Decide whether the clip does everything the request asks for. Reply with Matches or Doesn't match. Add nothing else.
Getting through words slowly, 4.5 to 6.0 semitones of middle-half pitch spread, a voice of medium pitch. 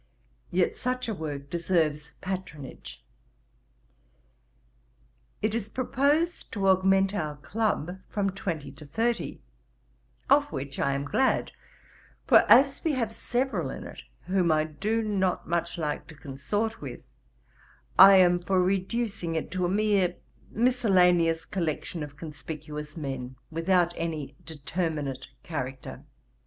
Matches